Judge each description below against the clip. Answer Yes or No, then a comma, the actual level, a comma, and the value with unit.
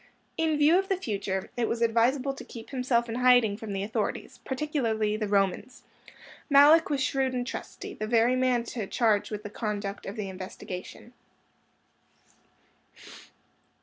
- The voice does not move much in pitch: No, average, 3.9 semitones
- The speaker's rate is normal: Yes, average, 150 wpm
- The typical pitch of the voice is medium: No, high, 235 Hz